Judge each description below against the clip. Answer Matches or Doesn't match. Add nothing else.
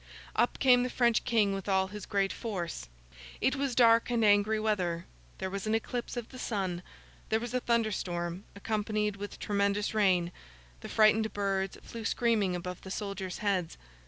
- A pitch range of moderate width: Matches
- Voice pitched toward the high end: Matches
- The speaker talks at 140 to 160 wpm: Doesn't match